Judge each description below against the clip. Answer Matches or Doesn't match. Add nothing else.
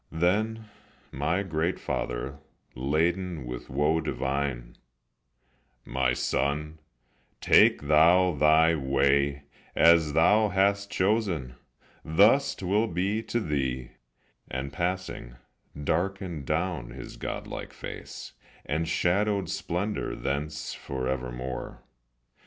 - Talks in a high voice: Doesn't match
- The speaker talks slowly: Matches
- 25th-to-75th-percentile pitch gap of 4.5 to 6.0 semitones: Matches